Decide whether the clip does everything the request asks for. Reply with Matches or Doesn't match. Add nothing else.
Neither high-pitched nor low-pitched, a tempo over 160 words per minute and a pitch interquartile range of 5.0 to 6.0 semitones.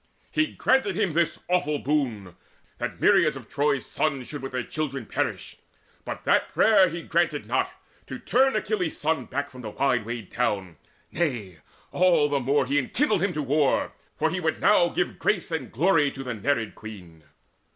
Matches